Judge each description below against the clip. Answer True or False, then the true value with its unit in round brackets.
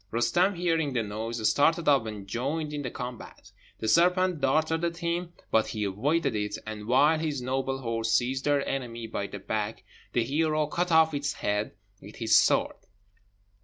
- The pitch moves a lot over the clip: True (6.1 semitones)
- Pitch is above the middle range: False (135 Hz)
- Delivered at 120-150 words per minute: False (175 wpm)